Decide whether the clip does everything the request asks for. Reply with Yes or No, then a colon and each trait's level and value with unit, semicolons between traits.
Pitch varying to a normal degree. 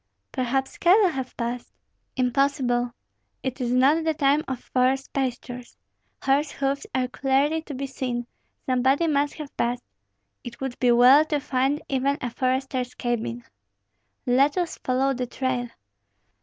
No: narrow, 2.1 semitones